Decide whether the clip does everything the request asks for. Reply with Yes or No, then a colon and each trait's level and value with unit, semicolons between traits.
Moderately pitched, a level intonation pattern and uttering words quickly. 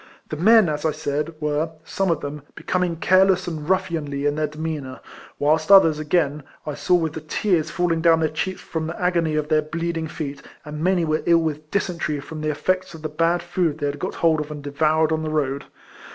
Yes: medium, 160 Hz; narrow, 2.2 semitones; fast, 225 wpm